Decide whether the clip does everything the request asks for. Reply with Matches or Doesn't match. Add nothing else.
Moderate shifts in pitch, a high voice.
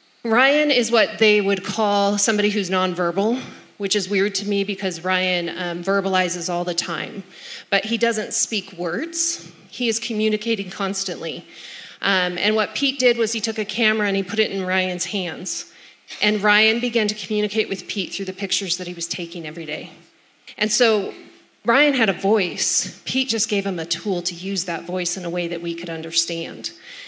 Matches